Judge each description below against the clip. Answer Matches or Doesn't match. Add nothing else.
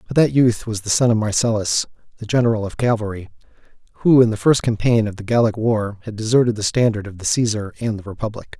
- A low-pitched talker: Matches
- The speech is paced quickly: Matches